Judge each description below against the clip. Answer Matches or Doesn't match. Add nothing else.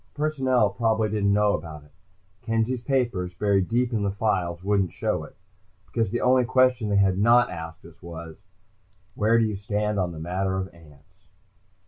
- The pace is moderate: Matches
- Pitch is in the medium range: Doesn't match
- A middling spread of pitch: Matches